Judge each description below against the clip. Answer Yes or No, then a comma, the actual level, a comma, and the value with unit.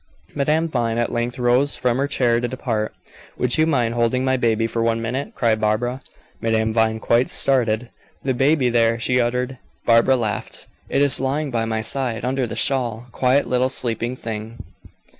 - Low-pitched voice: Yes, low, 120 Hz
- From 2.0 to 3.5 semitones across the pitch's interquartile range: Yes, narrow, 2.4 semitones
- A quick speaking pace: No, average, 180 wpm